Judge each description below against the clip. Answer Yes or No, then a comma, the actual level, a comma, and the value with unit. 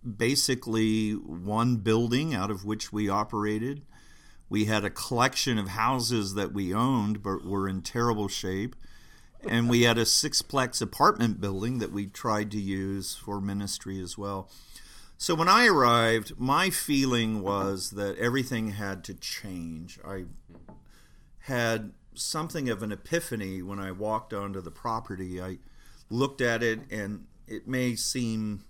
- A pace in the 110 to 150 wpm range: Yes, average, 145 wpm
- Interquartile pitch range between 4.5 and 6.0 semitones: No, average, 3.3 semitones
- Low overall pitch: Yes, low, 105 Hz